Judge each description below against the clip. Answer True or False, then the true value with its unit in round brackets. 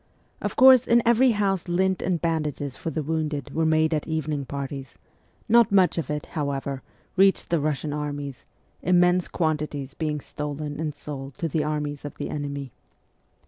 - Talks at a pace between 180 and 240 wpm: False (165 wpm)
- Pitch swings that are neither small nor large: True (3.3 semitones)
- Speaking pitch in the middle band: True (155 Hz)